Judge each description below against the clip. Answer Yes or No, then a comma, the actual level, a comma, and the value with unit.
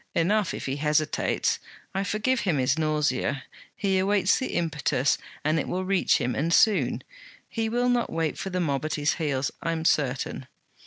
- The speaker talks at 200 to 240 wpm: No, average, 180 wpm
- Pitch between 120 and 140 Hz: No, medium, 165 Hz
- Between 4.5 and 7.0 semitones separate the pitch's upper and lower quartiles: Yes, average, 5.0 semitones